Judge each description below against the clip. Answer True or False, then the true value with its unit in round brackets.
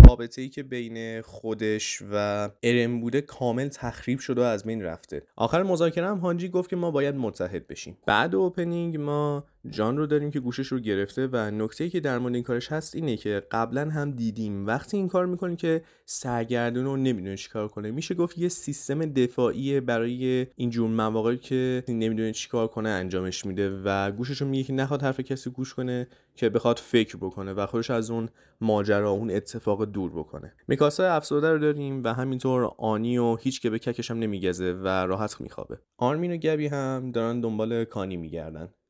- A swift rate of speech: True (190 wpm)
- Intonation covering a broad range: False (4.2 semitones)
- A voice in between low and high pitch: False (120 Hz)